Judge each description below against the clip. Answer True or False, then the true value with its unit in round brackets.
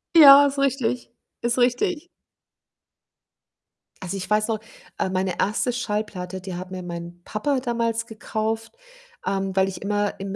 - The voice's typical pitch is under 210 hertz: False (215 Hz)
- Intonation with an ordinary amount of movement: True (4.4 semitones)